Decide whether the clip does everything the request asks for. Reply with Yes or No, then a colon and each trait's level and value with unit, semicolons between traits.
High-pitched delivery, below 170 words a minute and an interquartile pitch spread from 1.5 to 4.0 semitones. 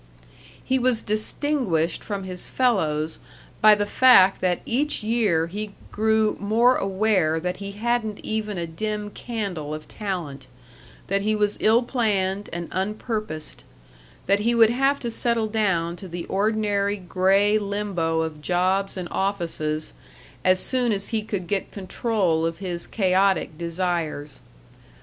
Yes: high, 200 Hz; average, 140 wpm; average, 3.7 semitones